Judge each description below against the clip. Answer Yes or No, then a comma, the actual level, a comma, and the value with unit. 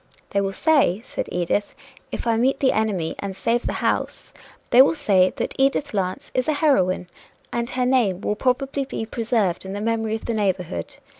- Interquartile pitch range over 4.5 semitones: Yes, average, 5.1 semitones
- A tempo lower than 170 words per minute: No, average, 195 wpm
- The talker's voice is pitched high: Yes, high, 225 Hz